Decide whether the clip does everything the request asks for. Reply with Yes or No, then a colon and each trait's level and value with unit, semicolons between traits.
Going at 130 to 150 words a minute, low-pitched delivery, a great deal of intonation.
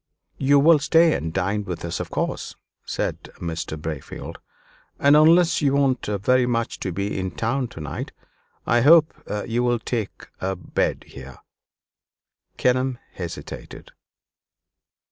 Yes: slow, 135 wpm; low, 120 Hz; wide, 7.0 semitones